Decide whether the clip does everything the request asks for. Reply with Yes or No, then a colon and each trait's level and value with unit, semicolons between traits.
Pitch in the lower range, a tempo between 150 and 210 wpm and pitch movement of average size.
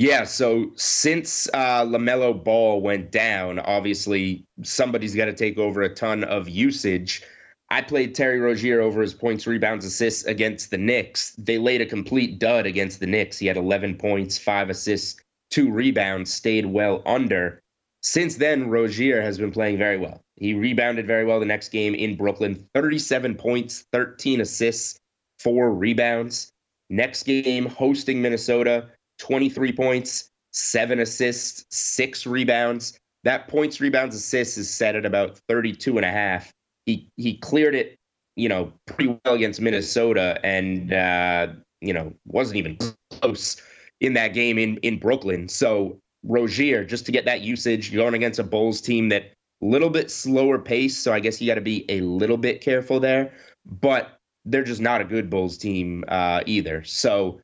Yes: low, 115 Hz; average, 165 wpm; average, 3.2 semitones